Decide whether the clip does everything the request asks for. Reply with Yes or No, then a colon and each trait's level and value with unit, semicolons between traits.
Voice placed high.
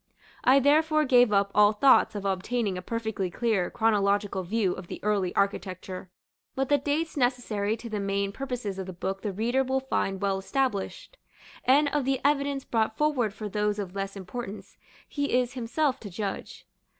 Yes: high, 220 Hz